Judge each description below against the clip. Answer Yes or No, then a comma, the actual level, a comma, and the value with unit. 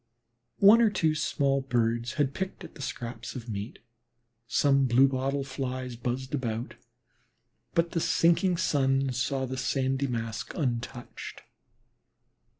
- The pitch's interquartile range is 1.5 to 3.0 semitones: Yes, narrow, 2.6 semitones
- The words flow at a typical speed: No, slow, 130 wpm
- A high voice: No, low, 130 Hz